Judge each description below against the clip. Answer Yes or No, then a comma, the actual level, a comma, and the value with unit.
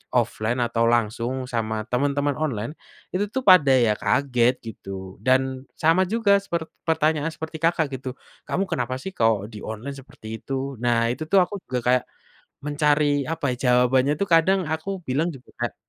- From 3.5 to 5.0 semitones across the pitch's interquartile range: Yes, average, 4.7 semitones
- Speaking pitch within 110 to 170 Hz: Yes, low, 135 Hz